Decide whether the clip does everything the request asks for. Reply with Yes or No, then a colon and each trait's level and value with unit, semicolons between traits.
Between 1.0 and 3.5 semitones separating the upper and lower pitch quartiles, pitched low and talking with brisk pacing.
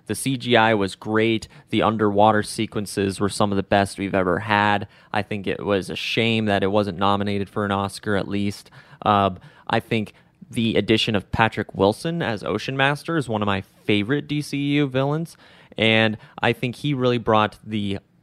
No: average, 2.8 semitones; low, 110 Hz; average, 180 wpm